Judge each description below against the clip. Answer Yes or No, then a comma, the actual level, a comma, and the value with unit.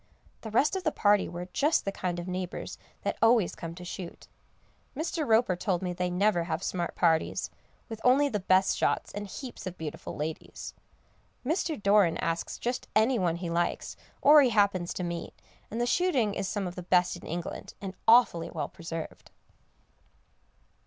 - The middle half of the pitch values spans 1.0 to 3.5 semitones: No, average, 5.0 semitones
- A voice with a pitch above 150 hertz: Yes, high, 190 Hz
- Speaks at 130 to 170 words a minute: No, average, 180 wpm